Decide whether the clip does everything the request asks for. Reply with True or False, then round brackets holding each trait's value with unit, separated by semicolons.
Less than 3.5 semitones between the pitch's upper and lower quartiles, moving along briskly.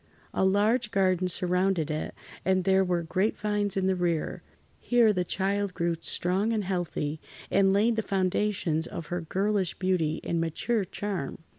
False (2.6 semitones; 155 wpm)